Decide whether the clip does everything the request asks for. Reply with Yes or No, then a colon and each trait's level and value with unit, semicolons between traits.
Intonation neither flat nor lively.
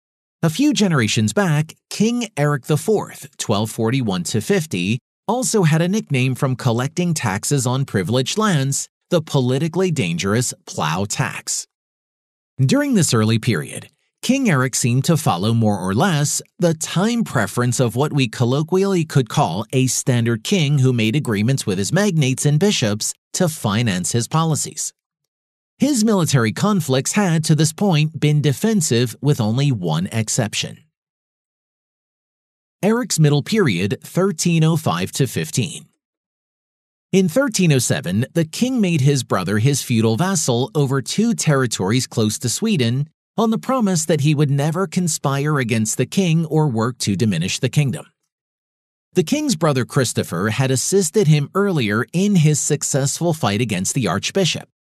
No: wide, 6.6 semitones